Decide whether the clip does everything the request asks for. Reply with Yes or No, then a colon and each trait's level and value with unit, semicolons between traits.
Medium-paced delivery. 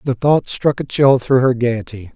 No: fast, 225 wpm